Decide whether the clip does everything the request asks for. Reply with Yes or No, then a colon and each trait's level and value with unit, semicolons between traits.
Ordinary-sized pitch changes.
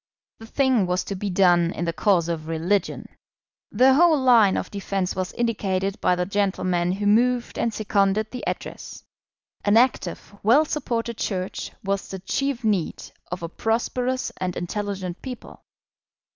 Yes: average, 4.2 semitones